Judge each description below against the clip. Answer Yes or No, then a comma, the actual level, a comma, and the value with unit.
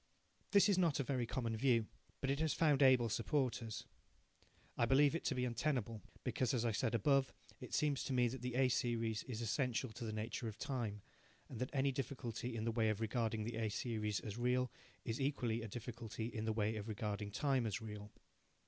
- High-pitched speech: No, low, 120 Hz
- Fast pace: Yes, fast, 210 wpm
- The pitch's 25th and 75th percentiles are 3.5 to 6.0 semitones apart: No, average, 3.1 semitones